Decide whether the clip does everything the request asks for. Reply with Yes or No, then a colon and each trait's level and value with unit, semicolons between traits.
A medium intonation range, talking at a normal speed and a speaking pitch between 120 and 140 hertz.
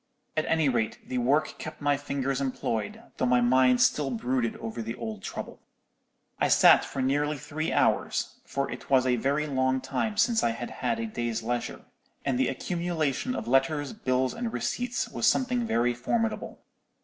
Yes: average, 4.1 semitones; average, 175 wpm; low, 135 Hz